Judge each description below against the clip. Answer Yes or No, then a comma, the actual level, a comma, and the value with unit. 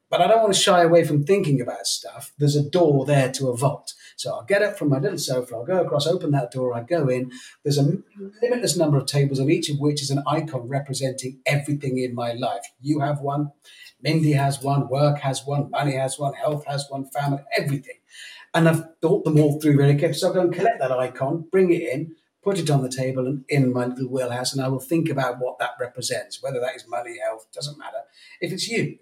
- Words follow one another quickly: Yes, fast, 240 wpm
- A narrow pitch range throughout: No, average, 3.6 semitones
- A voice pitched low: No, medium, 145 Hz